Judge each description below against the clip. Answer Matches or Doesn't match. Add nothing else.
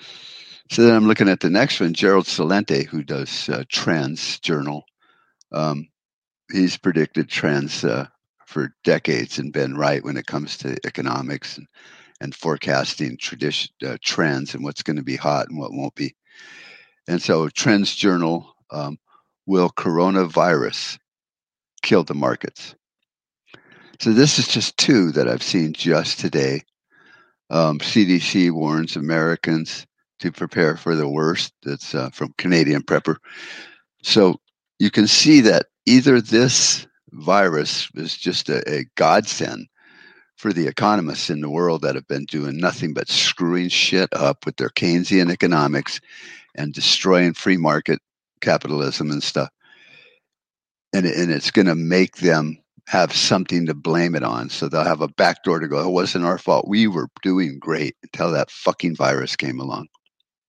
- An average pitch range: Matches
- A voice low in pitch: Matches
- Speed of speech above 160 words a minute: Doesn't match